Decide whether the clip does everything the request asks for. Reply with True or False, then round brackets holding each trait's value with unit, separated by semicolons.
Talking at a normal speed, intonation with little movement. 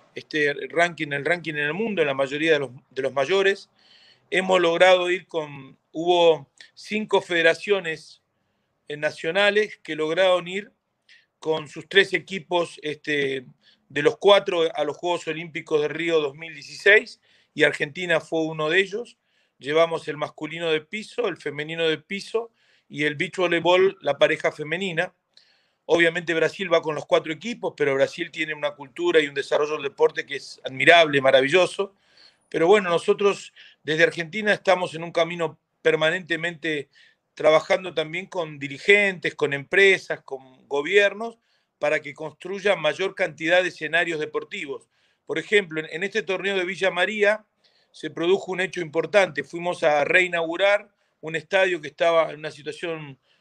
False (150 wpm; 3.8 semitones)